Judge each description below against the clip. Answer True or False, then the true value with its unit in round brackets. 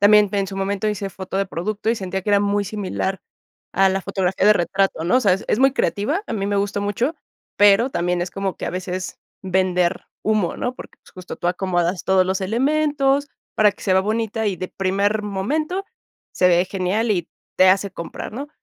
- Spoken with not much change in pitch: True (2.3 semitones)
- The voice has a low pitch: False (195 Hz)